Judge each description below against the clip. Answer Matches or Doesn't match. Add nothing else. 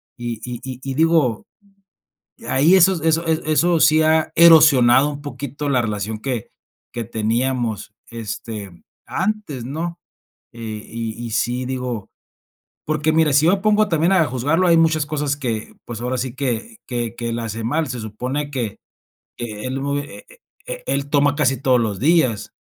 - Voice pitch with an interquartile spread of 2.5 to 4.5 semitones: Doesn't match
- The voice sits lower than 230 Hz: Matches